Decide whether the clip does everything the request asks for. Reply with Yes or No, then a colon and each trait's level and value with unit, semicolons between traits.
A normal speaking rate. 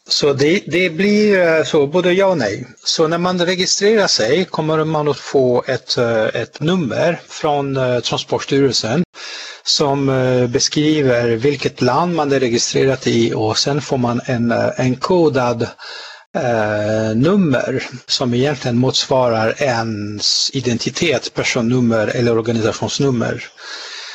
No: slow, 120 wpm